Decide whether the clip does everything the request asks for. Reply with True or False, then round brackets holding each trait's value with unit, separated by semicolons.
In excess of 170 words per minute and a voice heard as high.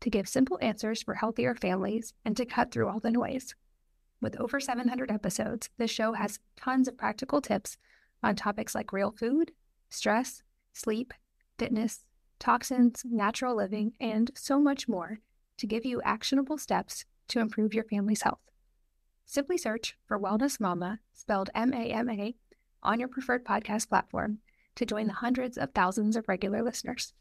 False (155 wpm; 230 Hz)